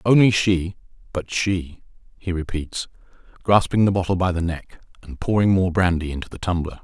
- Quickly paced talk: No, average, 160 wpm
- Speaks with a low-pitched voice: Yes, very low, 90 Hz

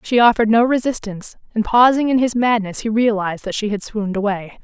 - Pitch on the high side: Yes, high, 220 Hz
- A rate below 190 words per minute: No, fast, 205 wpm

